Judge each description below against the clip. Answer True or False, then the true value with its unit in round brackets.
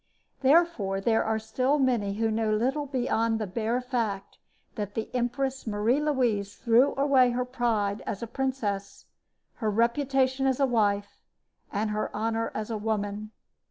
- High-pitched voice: True (230 Hz)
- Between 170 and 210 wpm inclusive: False (155 wpm)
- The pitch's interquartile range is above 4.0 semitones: False (3.6 semitones)